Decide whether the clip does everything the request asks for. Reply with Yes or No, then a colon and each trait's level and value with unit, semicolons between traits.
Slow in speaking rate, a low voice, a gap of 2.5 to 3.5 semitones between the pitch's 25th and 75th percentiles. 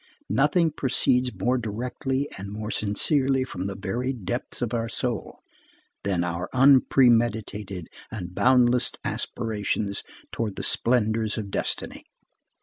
No: slow, 120 wpm; low, 115 Hz; average, 4.0 semitones